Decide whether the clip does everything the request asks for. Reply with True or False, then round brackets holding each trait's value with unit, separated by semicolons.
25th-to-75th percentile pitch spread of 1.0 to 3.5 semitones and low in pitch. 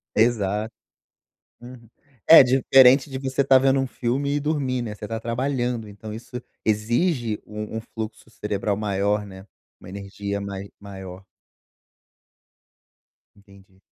False (4.0 semitones; 110 Hz)